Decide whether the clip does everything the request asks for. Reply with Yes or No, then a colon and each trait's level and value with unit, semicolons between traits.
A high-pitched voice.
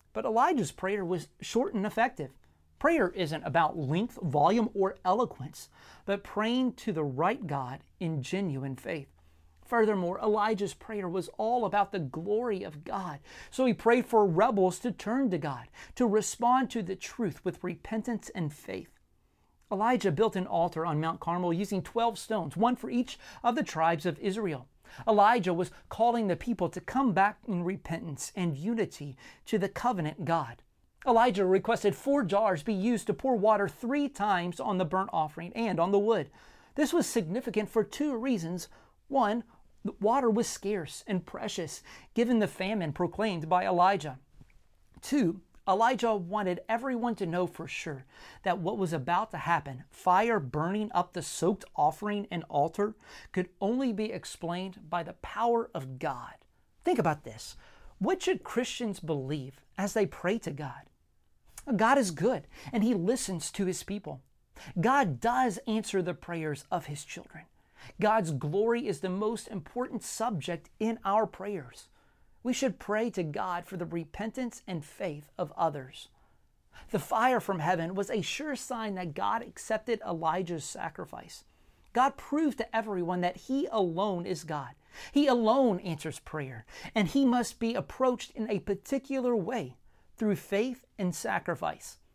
Yes: high, 200 Hz